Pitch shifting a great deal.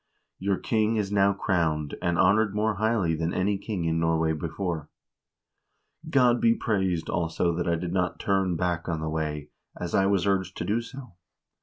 No: average, 3.5 semitones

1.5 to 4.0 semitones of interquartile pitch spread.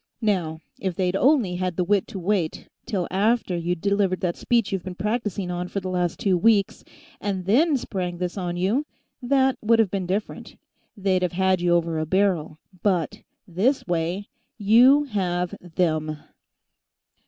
Yes: average, 2.9 semitones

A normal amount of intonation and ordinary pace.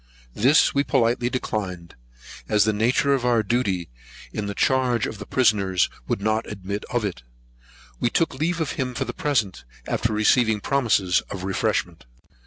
Yes: average, 4.0 semitones; average, 165 wpm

